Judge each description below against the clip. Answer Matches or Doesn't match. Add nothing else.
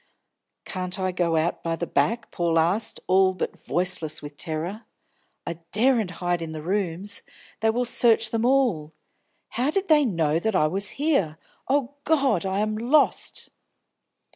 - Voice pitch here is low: Doesn't match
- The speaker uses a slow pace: Doesn't match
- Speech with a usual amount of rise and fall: Doesn't match